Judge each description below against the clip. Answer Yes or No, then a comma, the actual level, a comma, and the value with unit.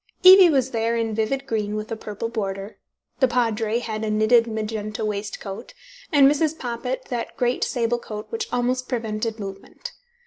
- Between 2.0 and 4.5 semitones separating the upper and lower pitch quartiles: Yes, average, 2.9 semitones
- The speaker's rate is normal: Yes, average, 165 wpm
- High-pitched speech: Yes, high, 230 Hz